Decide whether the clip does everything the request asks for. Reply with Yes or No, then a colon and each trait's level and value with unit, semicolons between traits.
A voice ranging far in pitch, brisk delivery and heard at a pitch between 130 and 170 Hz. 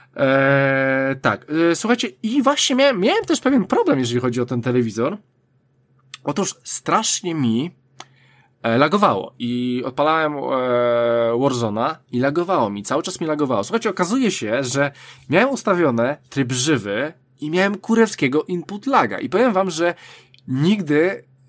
No: wide, 6.7 semitones; average, 140 wpm; medium, 140 Hz